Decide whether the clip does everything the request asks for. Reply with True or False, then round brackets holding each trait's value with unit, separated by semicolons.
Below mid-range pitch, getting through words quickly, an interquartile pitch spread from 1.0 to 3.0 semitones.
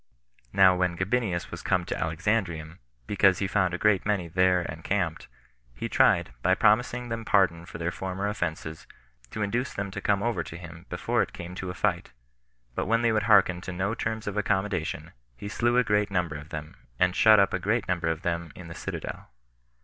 False (95 Hz; 210 wpm; 3.4 semitones)